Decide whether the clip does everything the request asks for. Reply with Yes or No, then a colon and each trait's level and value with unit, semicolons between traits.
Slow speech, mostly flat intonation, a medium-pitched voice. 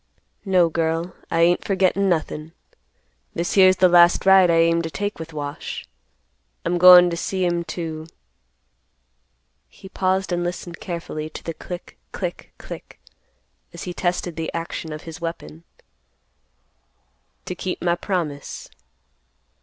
Yes: slow, 130 wpm; narrow, 2.3 semitones; medium, 170 Hz